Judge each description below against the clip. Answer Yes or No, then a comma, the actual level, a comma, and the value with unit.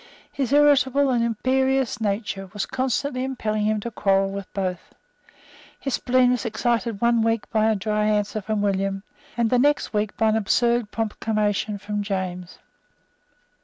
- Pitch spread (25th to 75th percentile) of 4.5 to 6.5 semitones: No, average, 3.3 semitones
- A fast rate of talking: No, average, 155 wpm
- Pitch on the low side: No, high, 220 Hz